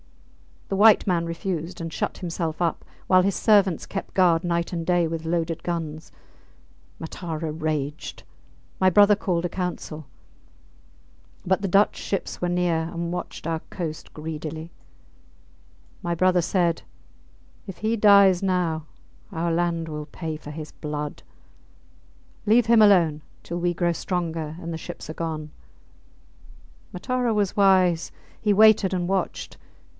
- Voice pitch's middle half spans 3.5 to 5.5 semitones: No, average, 2.7 semitones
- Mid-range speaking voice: Yes, medium, 170 Hz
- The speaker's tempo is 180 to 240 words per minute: No, average, 140 wpm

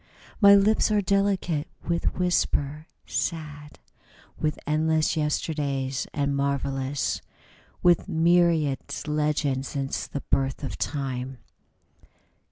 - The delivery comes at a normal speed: No, slow, 95 wpm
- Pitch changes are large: No, average, 3.4 semitones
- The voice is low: No, medium, 150 Hz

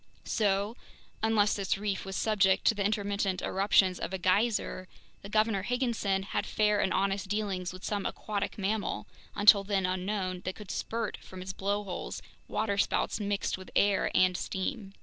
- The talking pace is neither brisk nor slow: Yes, average, 160 wpm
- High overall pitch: Yes, high, 200 Hz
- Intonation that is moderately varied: No, narrow, 1.8 semitones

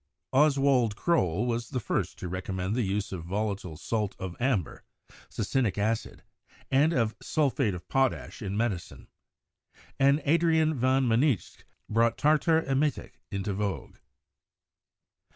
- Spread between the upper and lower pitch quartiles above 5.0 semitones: Yes, wide, 5.5 semitones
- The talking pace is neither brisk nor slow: No, slow, 125 wpm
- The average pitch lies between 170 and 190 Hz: No, low, 115 Hz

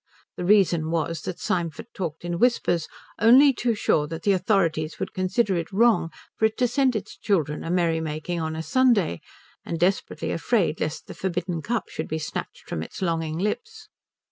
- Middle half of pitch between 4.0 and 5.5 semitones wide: Yes, average, 4.9 semitones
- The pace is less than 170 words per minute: No, average, 180 wpm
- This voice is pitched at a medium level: Yes, medium, 175 Hz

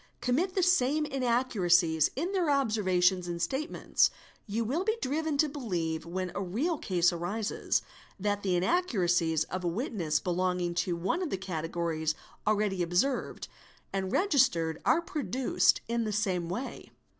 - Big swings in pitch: Yes, wide, 7.5 semitones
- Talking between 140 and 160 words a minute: Yes, average, 145 wpm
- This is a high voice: Yes, high, 200 Hz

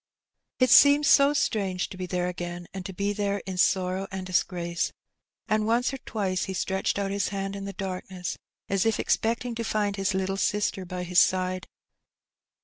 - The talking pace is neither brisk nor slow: Yes, average, 185 wpm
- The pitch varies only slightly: Yes, narrow, 2.2 semitones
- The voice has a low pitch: No, high, 195 Hz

